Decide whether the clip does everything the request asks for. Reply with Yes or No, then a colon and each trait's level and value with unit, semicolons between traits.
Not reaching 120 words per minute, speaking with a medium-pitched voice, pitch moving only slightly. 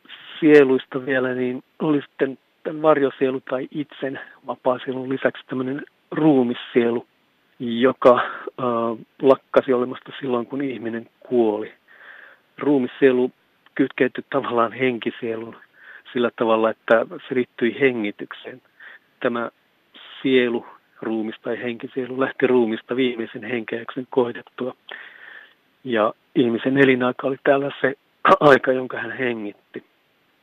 No: average, 100 wpm; low, 130 Hz; narrow, 2.2 semitones